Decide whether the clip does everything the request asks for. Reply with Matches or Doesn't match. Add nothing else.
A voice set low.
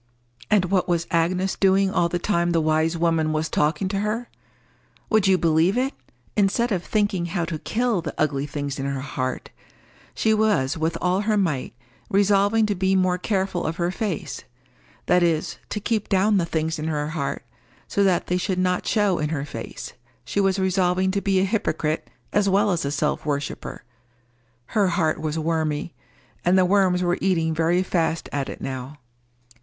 Doesn't match